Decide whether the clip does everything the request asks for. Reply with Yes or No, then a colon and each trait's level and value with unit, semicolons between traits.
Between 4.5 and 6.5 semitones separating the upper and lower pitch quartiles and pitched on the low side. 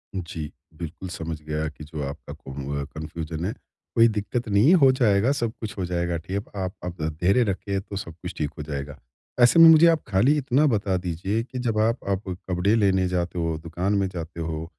Yes: average, 5.2 semitones; very low, 95 Hz